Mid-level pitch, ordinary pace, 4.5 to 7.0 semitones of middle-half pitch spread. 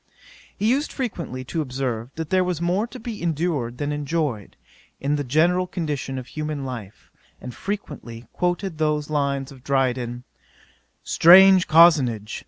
Yes: medium, 150 Hz; average, 145 wpm; wide, 5.4 semitones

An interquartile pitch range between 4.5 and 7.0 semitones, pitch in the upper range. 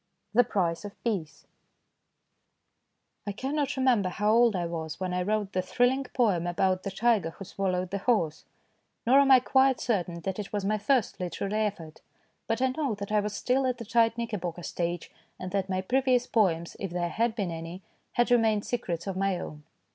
Yes: average, 4.9 semitones; high, 205 Hz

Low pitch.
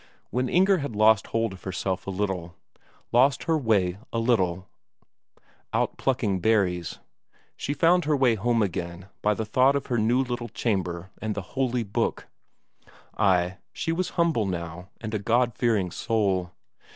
Yes: low, 110 Hz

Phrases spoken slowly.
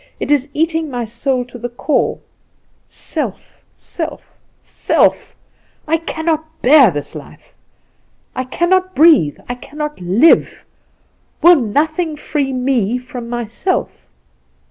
Yes: slow, 115 wpm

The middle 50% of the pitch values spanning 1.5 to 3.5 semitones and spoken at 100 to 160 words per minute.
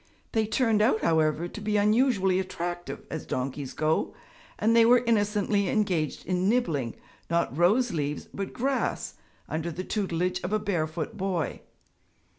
No: average, 4.6 semitones; average, 145 wpm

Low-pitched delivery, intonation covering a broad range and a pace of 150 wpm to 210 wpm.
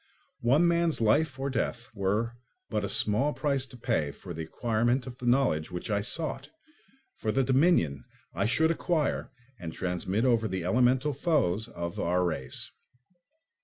Yes: low, 120 Hz; wide, 6.5 semitones; average, 160 wpm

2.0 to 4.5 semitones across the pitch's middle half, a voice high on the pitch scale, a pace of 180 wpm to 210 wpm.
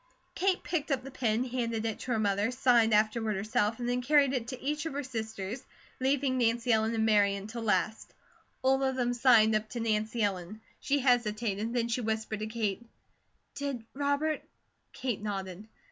Yes: average, 3.2 semitones; high, 230 Hz; average, 185 wpm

